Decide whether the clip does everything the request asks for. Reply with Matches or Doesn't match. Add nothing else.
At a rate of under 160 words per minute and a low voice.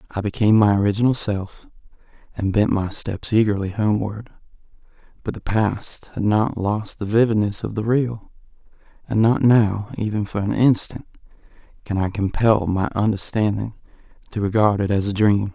Matches